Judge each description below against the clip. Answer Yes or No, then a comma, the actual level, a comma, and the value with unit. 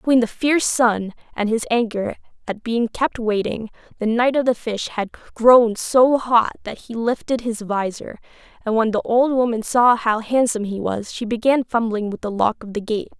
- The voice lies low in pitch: No, high, 230 Hz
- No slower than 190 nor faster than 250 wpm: Yes, average, 200 wpm